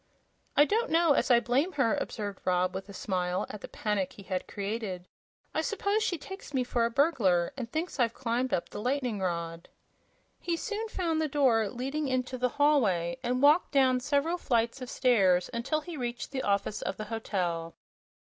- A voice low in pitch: No, high, 245 Hz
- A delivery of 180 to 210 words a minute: Yes, average, 190 wpm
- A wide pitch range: Yes, wide, 6.4 semitones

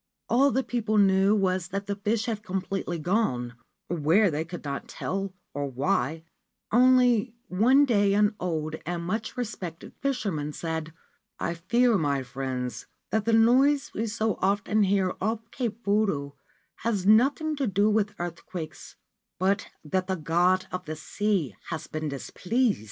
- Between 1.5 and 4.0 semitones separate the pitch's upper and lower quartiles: No, average, 5.1 semitones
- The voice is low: No, high, 195 Hz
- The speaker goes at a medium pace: Yes, average, 155 wpm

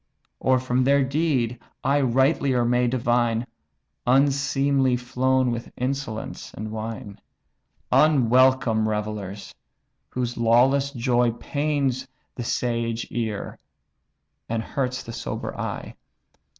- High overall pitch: No, low, 125 Hz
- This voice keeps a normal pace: No, slow, 100 wpm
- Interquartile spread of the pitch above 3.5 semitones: No, narrow, 2.5 semitones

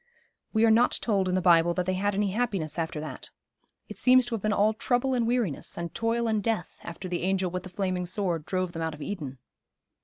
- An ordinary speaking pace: No, fast, 235 wpm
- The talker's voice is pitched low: No, high, 190 Hz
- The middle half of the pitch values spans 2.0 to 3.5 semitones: No, average, 4.3 semitones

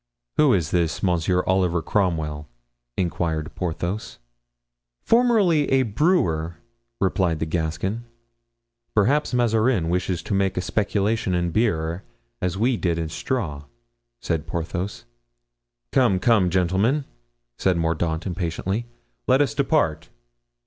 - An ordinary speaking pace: No, slow, 115 wpm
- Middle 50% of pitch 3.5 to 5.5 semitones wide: Yes, average, 5.2 semitones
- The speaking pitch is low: Yes, very low, 95 Hz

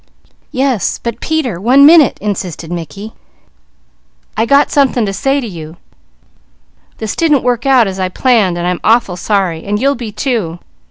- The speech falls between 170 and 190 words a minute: No, average, 160 wpm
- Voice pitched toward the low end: No, high, 220 Hz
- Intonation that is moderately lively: No, wide, 6.2 semitones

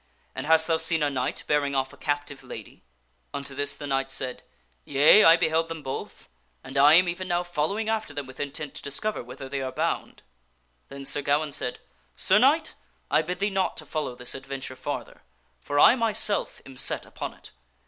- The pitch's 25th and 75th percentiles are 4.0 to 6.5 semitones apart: No, average, 3.5 semitones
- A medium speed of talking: No, fast, 210 wpm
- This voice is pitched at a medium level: Yes, medium, 145 Hz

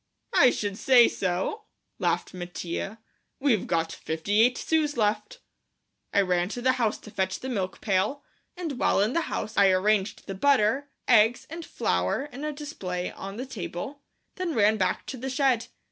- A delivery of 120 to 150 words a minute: No, average, 175 wpm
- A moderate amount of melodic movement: No, wide, 6.0 semitones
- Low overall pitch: No, high, 215 Hz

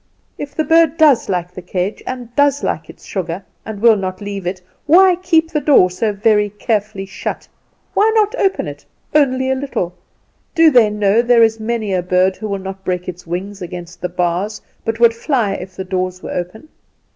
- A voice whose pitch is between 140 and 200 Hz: No, high, 210 Hz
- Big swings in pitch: Yes, wide, 5.9 semitones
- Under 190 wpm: No, average, 195 wpm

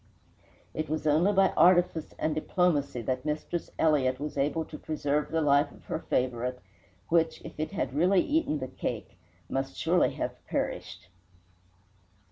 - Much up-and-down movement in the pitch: No, average, 3.4 semitones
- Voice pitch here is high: No, medium, 155 Hz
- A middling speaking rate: Yes, average, 150 wpm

